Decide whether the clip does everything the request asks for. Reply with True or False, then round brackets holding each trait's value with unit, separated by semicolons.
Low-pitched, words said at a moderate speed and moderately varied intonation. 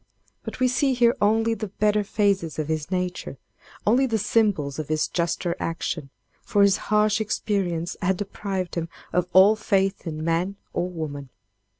False (190 Hz; 165 wpm; 4.1 semitones)